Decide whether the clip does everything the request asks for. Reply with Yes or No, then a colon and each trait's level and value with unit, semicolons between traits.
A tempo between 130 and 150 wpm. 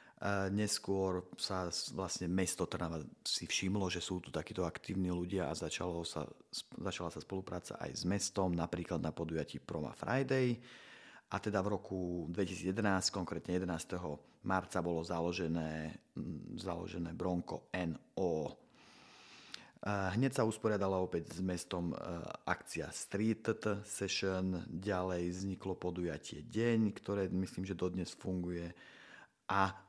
No: average, 120 wpm